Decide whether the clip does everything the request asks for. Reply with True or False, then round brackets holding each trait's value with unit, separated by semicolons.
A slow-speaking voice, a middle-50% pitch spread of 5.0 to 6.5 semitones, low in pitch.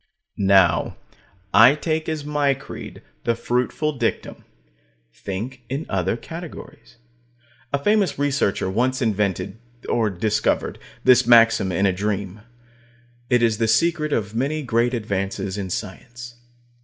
True (125 wpm; 5.5 semitones; 120 Hz)